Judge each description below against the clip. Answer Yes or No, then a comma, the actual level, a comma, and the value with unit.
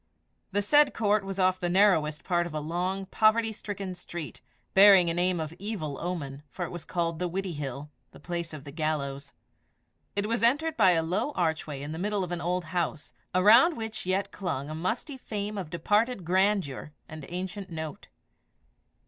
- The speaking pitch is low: No, medium, 180 Hz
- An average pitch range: Yes, average, 4.2 semitones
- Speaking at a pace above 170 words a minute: Yes, average, 180 wpm